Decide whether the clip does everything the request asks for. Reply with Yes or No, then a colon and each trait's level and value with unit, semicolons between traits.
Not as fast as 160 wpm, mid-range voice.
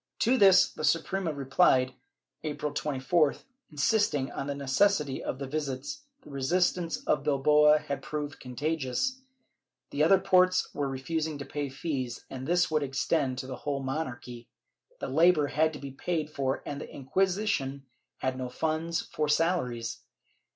Yes: average, 150 wpm; medium, 150 Hz